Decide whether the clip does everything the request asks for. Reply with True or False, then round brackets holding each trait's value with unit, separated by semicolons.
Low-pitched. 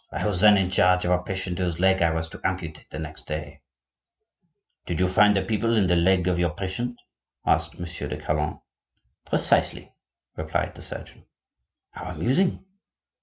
True (90 Hz)